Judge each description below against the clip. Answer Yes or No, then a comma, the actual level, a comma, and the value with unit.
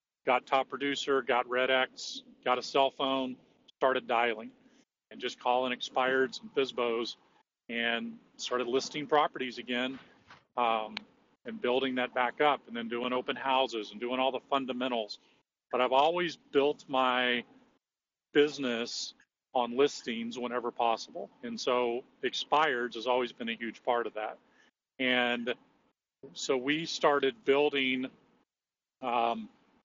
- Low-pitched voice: Yes, low, 125 Hz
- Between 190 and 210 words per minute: No, slow, 135 wpm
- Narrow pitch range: Yes, narrow, 2.0 semitones